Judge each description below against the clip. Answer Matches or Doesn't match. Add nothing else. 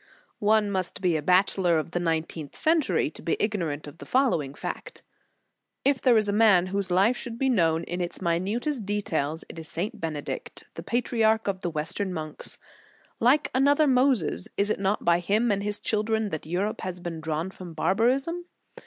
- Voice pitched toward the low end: Doesn't match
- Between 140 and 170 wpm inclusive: Doesn't match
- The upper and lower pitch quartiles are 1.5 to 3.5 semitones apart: Doesn't match